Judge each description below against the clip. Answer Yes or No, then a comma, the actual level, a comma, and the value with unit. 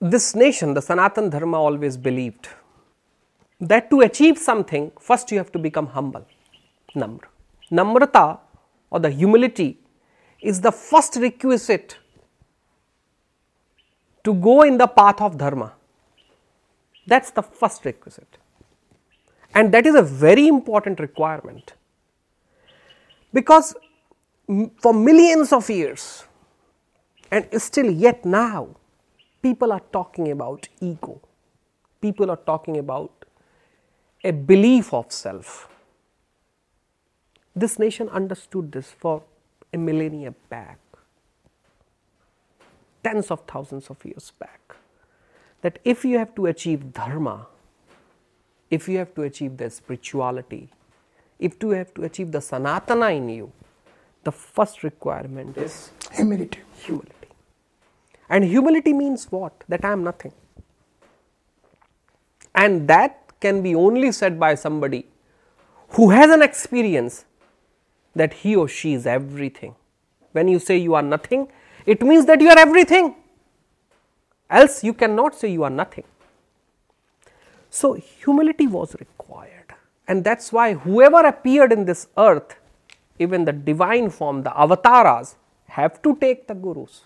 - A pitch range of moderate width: No, wide, 7.7 semitones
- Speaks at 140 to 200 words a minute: No, average, 120 wpm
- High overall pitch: Yes, high, 195 Hz